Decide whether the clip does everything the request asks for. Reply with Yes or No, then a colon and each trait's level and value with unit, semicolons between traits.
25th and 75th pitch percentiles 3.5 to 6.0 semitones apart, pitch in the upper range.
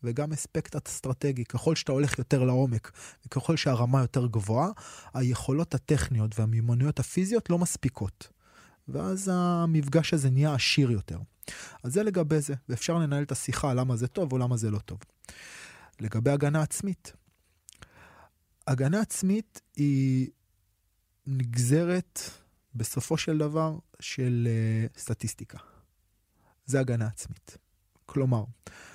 No: average, 5.1 semitones; low, 130 Hz